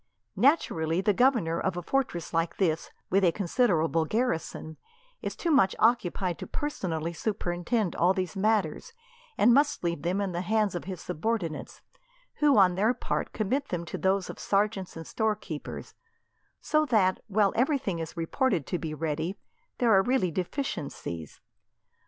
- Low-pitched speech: No, high, 190 Hz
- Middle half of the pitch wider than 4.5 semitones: Yes, average, 4.9 semitones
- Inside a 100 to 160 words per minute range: Yes, average, 155 wpm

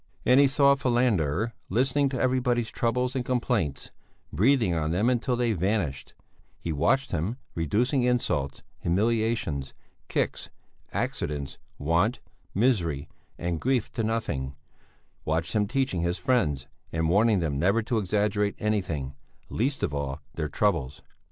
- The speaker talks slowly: Yes, slow, 130 wpm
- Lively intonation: Yes, wide, 7.2 semitones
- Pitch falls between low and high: No, low, 105 Hz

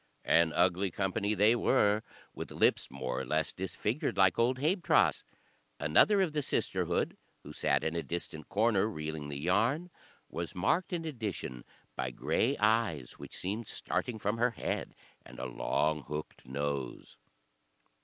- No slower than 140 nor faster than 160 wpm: Yes, average, 150 wpm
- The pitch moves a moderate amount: No, wide, 7.1 semitones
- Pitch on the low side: Yes, very low, 95 Hz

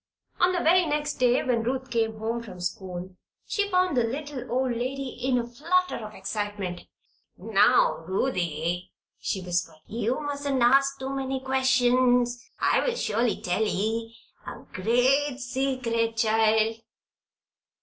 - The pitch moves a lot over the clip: No, average, 3.6 semitones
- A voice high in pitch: Yes, high, 245 Hz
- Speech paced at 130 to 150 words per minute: Yes, average, 140 wpm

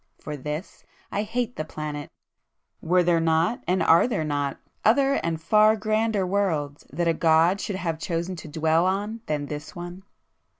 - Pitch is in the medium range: Yes, medium, 170 Hz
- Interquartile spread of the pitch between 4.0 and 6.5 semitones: Yes, average, 4.5 semitones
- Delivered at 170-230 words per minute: Yes, average, 175 wpm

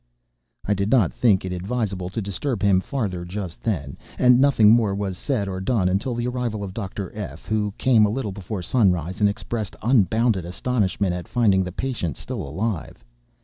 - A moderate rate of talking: Yes, average, 185 wpm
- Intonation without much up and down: No, average, 4.0 semitones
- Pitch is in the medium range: No, low, 100 Hz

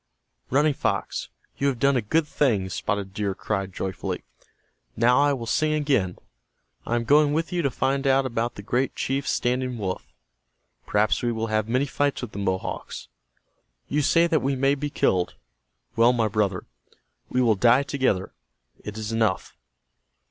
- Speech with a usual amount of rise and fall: Yes, average, 4.8 semitones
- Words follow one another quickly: No, average, 170 wpm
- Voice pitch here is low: Yes, low, 120 Hz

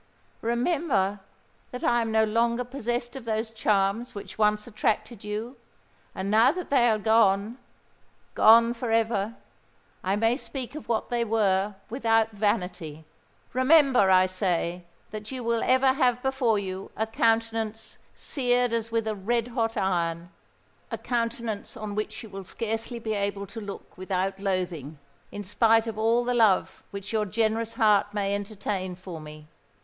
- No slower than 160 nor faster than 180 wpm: No, average, 150 wpm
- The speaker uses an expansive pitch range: No, average, 2.9 semitones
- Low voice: No, high, 220 Hz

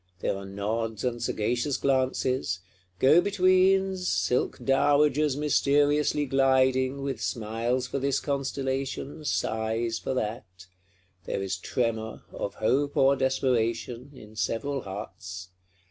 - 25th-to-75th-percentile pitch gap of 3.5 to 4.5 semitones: Yes, average, 4.0 semitones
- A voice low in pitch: Yes, low, 130 Hz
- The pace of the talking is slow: Yes, slow, 115 wpm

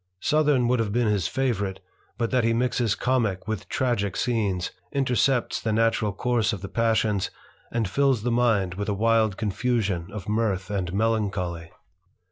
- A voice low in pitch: Yes, low, 110 Hz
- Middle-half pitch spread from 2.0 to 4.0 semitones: Yes, average, 3.4 semitones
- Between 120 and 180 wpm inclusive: Yes, average, 160 wpm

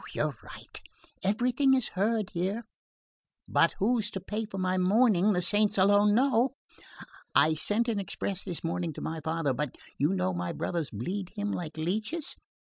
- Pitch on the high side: Yes, high, 195 Hz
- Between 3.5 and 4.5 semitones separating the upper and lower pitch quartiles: Yes, average, 4.2 semitones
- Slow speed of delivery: No, average, 165 wpm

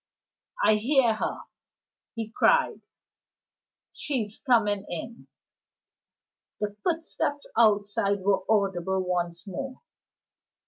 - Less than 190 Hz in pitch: No, high, 210 Hz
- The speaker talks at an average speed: No, slow, 85 wpm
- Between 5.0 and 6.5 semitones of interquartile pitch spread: No, average, 3.6 semitones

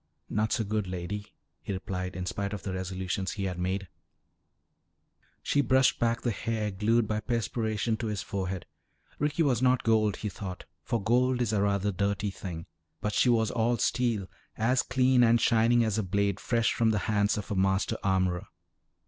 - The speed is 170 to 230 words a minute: Yes, average, 180 wpm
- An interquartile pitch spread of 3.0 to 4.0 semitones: Yes, average, 3.3 semitones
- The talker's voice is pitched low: Yes, low, 105 Hz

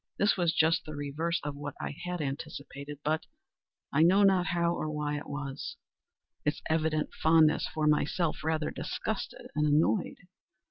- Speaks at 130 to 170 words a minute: Yes, average, 145 wpm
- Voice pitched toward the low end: No, medium, 155 Hz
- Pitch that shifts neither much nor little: No, narrow, 2.3 semitones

